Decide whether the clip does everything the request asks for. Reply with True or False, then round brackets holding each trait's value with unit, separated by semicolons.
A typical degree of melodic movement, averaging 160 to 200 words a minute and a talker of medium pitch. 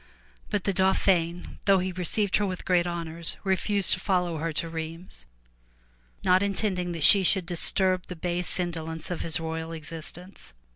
False (2.3 semitones; 165 wpm; 180 Hz)